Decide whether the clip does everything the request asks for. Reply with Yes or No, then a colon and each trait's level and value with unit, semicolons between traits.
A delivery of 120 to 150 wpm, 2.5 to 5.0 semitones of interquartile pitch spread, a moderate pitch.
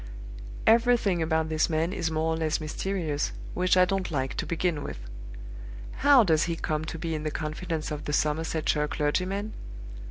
No: average, 170 wpm; average, 2.9 semitones; medium, 160 Hz